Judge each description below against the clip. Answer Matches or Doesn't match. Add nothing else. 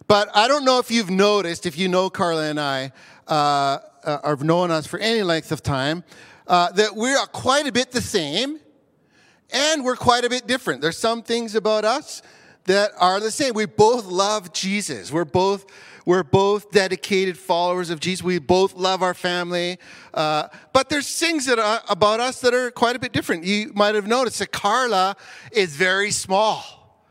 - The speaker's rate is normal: Matches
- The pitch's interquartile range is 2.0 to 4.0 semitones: Doesn't match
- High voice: Matches